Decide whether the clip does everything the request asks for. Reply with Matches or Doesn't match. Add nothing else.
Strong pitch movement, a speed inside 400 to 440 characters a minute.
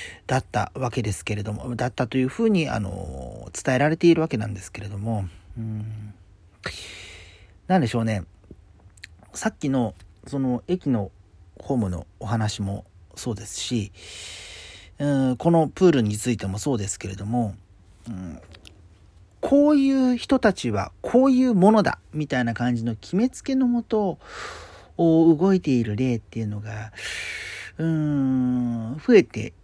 Doesn't match